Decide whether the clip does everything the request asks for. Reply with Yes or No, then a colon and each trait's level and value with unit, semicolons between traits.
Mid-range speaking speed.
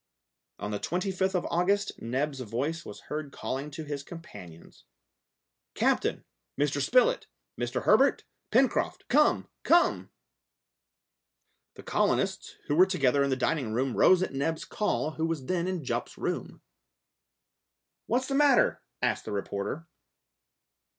No: slow, 130 wpm